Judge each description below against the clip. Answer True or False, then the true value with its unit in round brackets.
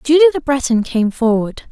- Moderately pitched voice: False (260 Hz)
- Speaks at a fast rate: False (175 wpm)